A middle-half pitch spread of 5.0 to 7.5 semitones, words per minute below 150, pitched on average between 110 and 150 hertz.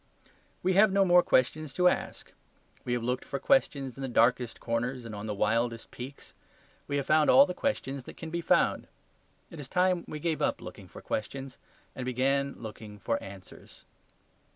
No: wide, 5.4 semitones; average, 190 wpm; low, 135 Hz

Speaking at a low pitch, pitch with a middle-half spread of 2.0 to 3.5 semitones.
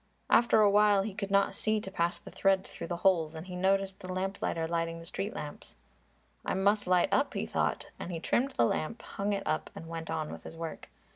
No: high, 190 Hz; average, 3.1 semitones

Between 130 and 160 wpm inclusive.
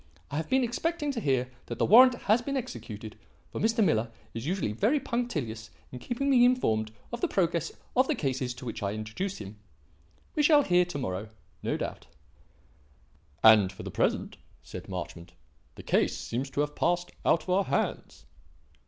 No: average, 180 wpm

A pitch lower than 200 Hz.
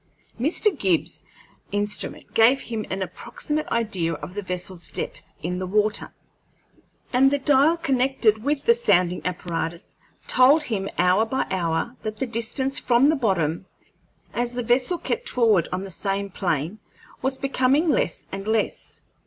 No: high, 220 Hz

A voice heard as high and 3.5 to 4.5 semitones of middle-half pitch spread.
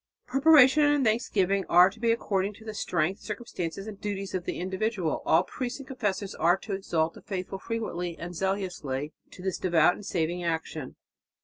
Yes: high, 195 Hz; average, 3.8 semitones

